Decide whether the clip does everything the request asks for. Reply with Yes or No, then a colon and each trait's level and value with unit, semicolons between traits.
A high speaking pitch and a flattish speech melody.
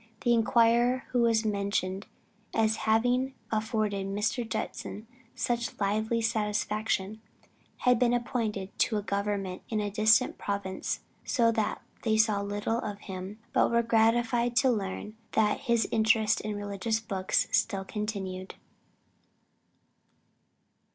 Yes: high, 220 Hz; narrow, 2.3 semitones